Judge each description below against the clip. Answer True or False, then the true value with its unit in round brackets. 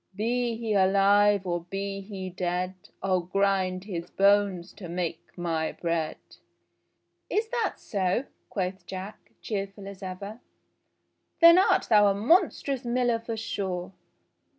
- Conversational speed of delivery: False (130 wpm)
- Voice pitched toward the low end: False (195 Hz)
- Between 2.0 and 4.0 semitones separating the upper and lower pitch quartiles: True (3.2 semitones)